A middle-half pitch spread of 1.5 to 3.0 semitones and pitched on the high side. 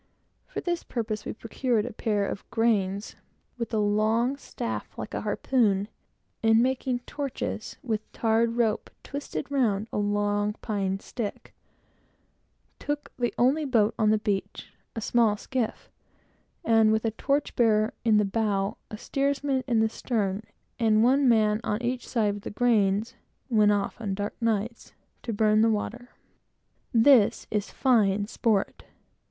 Yes: average, 2.7 semitones; high, 220 Hz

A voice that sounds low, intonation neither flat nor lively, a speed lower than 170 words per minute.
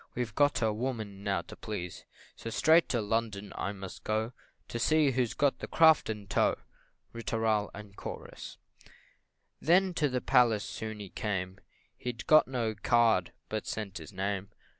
Yes: low, 110 Hz; average, 3.6 semitones; average, 160 wpm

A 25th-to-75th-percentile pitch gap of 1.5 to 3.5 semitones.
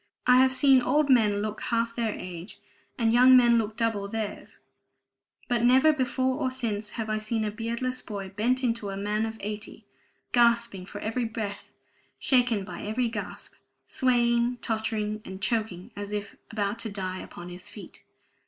Yes: average, 2.9 semitones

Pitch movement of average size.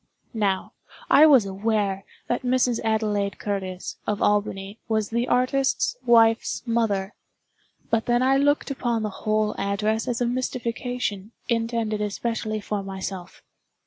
Yes: average, 3.0 semitones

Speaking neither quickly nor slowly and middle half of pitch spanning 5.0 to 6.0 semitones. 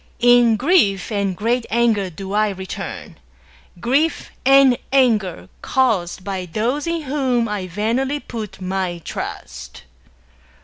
No: slow, 130 wpm; average, 5.3 semitones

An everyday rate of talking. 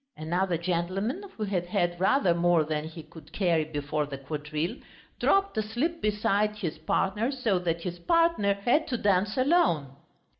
Yes: average, 155 wpm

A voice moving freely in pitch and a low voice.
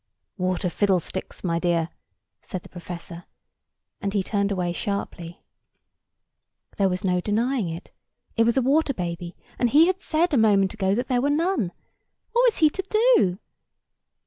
No: wide, 7.2 semitones; high, 200 Hz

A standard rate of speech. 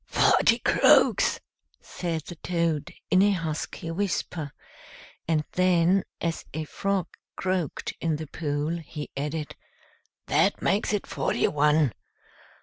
No: slow, 120 wpm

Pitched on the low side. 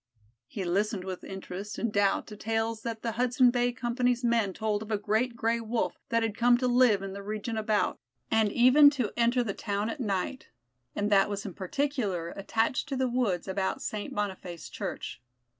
No: high, 220 Hz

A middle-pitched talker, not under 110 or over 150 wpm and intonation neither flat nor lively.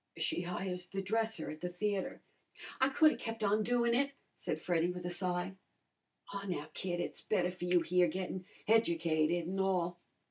No: medium, 180 Hz; average, 180 wpm; average, 3.0 semitones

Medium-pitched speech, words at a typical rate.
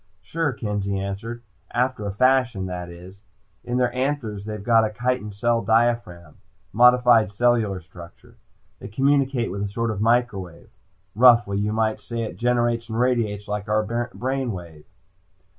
No: low, 115 Hz; average, 150 wpm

